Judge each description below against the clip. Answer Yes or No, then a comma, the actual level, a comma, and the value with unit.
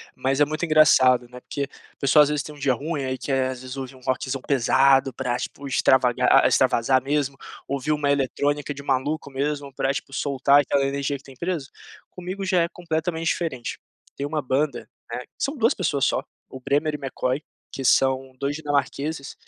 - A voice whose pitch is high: No, medium, 140 Hz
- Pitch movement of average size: No, narrow, 2.2 semitones